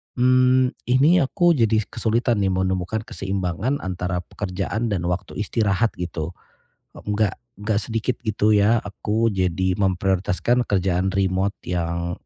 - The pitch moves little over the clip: No, average, 3.8 semitones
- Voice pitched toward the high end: No, low, 100 Hz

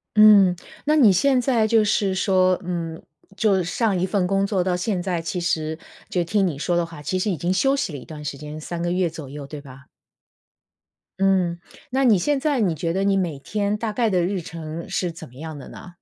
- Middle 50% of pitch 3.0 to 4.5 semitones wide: Yes, average, 3.8 semitones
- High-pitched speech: No, medium, 180 Hz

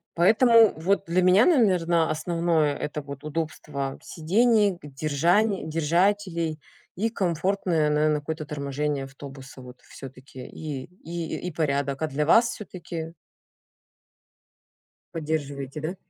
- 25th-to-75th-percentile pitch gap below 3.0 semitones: No, average, 4.0 semitones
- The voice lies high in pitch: No, medium, 160 Hz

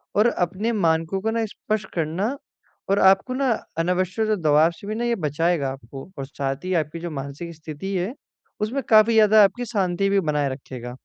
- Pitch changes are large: Yes, wide, 5.9 semitones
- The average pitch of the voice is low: No, medium, 180 Hz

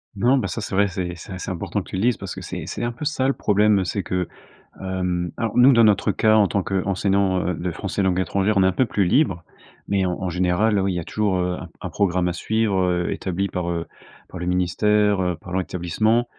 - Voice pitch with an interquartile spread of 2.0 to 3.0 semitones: Yes, average, 2.7 semitones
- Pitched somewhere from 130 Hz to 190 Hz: No, very low, 95 Hz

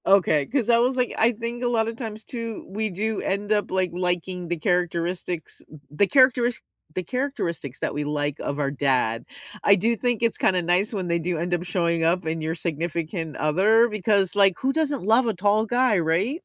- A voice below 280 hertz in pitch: Yes, high, 190 Hz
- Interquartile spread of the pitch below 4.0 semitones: No, average, 5.2 semitones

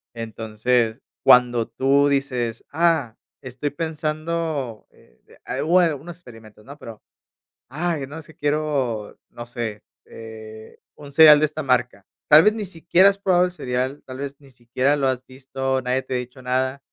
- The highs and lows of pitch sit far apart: No, average, 4.1 semitones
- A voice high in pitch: No, low, 135 Hz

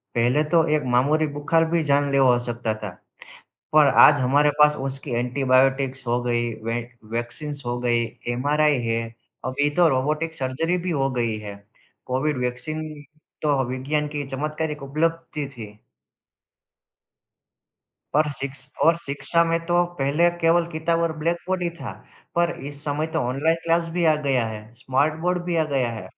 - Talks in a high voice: No, medium, 145 Hz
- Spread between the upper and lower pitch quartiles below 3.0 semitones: No, average, 3.8 semitones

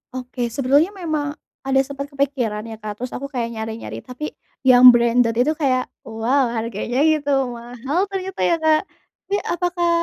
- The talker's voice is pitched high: Yes, very high, 255 Hz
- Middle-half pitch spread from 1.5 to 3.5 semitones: No, average, 3.9 semitones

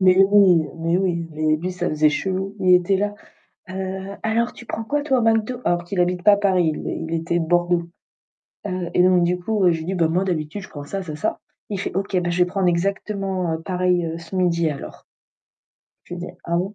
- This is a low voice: No, medium, 180 Hz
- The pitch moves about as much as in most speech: No, narrow, 2.3 semitones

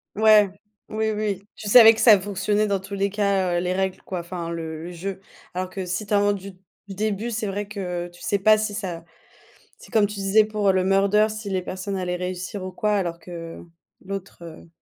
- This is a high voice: Yes, high, 195 Hz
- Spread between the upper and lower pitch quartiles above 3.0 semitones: No, narrow, 2.4 semitones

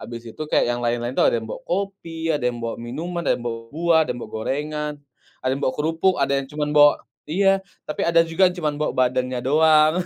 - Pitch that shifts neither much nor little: Yes, average, 4.6 semitones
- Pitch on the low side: No, medium, 150 Hz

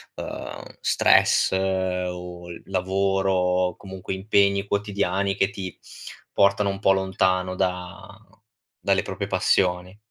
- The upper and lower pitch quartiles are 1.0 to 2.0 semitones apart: Yes, narrow, 1.4 semitones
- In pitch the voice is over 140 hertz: No, very low, 95 Hz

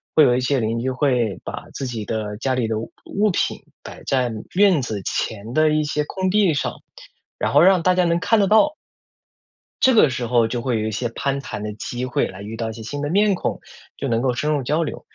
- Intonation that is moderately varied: No, wide, 6.3 semitones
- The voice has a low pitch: Yes, low, 130 Hz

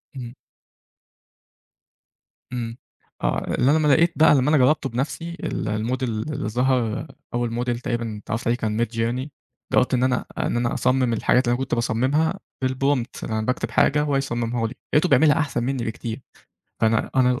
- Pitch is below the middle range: Yes, low, 125 Hz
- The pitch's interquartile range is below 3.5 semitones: Yes, average, 2.8 semitones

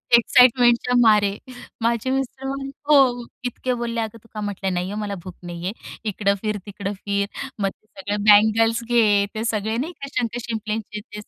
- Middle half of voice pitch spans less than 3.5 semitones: Yes, average, 2.8 semitones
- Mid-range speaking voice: No, high, 220 Hz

